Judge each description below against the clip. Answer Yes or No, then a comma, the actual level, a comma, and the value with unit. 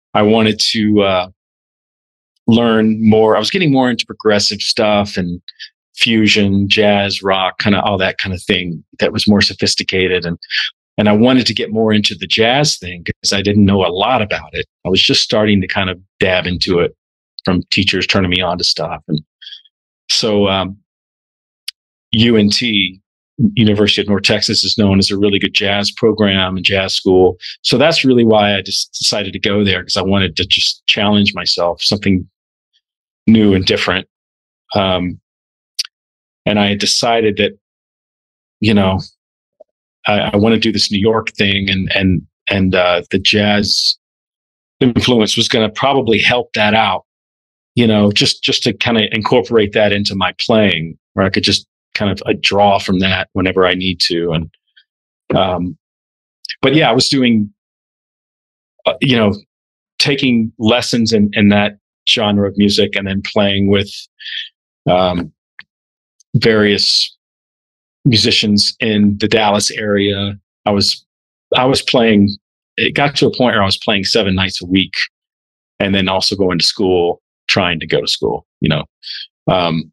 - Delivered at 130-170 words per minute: Yes, average, 165 wpm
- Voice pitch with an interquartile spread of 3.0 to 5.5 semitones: No, narrow, 2.5 semitones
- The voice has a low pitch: Yes, low, 100 Hz